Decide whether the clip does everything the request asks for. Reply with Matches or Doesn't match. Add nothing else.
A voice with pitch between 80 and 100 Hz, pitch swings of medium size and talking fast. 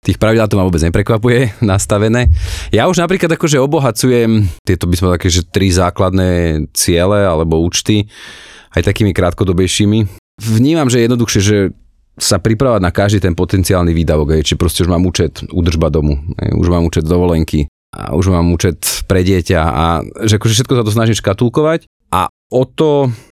Matches